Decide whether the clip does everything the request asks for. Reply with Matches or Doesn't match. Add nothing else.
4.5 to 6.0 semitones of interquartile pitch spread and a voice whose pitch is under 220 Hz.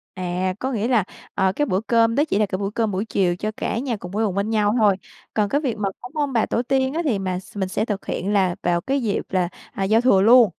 Doesn't match